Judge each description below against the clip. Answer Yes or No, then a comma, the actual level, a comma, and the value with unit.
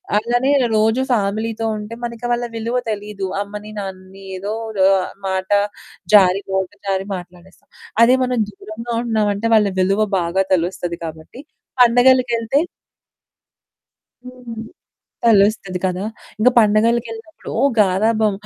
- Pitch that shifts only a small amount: No, average, 3.2 semitones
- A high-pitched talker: Yes, high, 210 Hz